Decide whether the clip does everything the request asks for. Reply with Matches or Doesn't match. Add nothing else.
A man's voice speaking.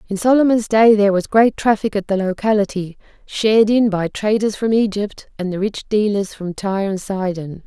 Doesn't match